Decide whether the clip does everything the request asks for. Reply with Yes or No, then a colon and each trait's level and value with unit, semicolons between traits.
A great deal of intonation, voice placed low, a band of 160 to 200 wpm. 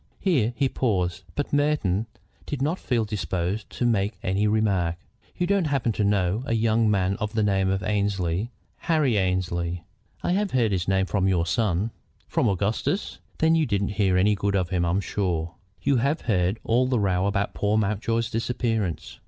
No: average, 3.8 semitones; low, 105 Hz; average, 180 wpm